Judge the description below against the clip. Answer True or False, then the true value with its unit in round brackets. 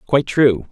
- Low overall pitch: True (120 Hz)